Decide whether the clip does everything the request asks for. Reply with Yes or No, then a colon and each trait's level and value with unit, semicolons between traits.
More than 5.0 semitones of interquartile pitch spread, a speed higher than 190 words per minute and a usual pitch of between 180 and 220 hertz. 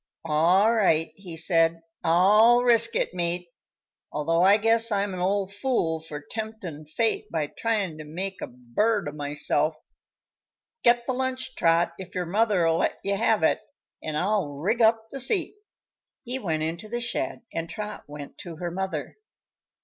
No: wide, 5.4 semitones; average, 165 wpm; high, 190 Hz